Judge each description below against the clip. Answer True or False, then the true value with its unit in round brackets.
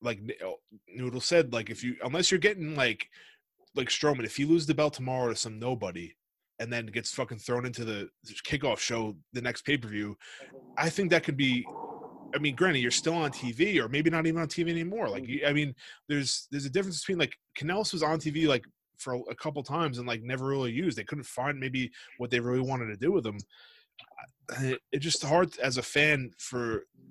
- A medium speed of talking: False (210 wpm)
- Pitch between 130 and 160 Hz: True (135 Hz)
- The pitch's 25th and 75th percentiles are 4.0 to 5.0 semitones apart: True (4.5 semitones)